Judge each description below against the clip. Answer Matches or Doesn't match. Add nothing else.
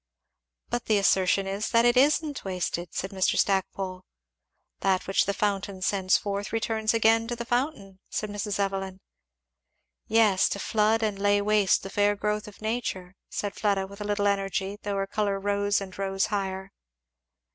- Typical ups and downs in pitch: Doesn't match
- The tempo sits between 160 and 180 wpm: Matches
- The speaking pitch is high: Matches